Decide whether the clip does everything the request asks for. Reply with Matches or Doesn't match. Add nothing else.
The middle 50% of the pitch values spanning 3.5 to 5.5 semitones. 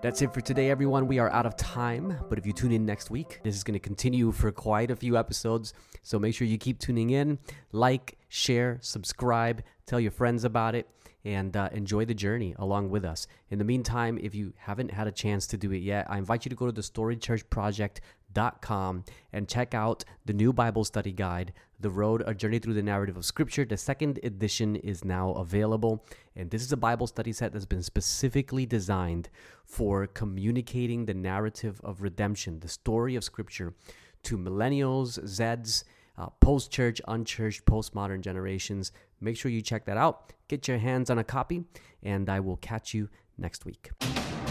Doesn't match